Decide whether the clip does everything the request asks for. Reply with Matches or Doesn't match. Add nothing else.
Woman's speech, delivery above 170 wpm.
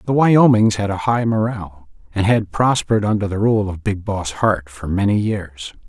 Doesn't match